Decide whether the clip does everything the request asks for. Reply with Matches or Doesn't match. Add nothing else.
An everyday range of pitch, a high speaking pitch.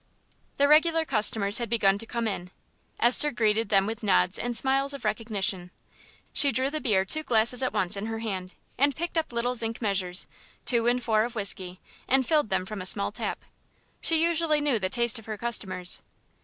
Matches